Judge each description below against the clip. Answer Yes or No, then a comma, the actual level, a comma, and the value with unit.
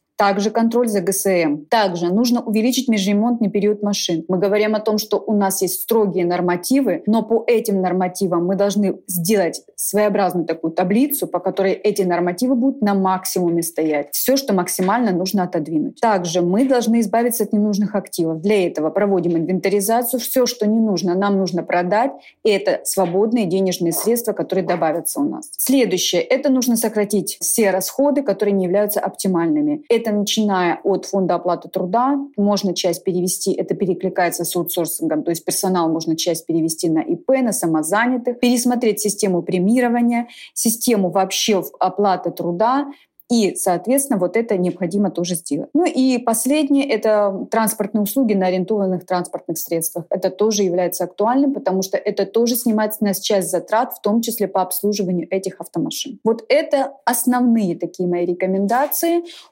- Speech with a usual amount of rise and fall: Yes, average, 4.2 semitones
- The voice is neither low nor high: No, high, 200 Hz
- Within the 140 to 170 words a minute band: Yes, average, 155 wpm